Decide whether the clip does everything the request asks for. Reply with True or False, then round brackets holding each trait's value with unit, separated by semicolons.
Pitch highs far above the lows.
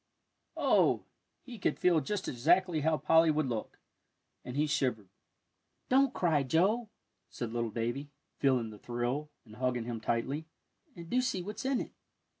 True (6.9 semitones)